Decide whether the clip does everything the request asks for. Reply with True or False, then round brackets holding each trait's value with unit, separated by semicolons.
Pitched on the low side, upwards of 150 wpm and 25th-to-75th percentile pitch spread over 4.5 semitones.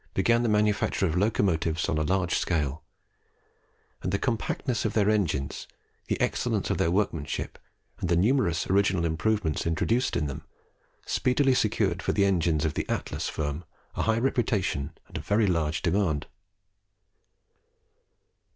False (95 Hz; 145 wpm; 5.2 semitones)